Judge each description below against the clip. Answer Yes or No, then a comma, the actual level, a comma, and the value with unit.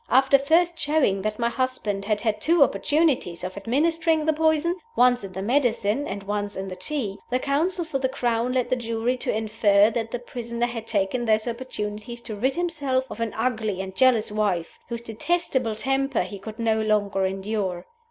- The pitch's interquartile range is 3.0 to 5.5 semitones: Yes, average, 4.4 semitones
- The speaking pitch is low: No, high, 235 Hz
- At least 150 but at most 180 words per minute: No, average, 190 wpm